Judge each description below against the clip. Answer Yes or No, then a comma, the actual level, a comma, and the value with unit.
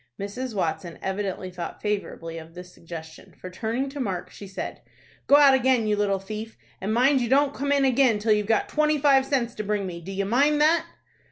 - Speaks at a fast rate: Yes, fast, 215 wpm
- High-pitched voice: Yes, high, 215 Hz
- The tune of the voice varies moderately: No, wide, 5.8 semitones